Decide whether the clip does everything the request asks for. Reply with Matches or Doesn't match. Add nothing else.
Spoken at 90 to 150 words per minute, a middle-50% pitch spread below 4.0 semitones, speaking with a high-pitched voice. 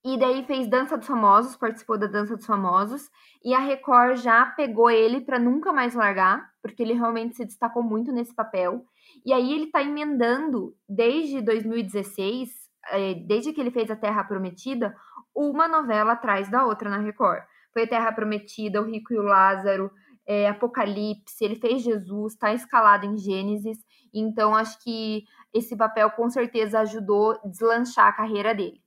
Doesn't match